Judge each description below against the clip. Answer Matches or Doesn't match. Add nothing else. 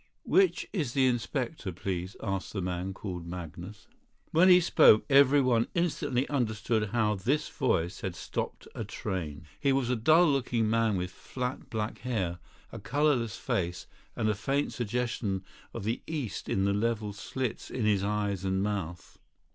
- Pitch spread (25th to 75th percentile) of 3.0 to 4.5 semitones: Doesn't match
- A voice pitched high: Doesn't match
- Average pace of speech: Matches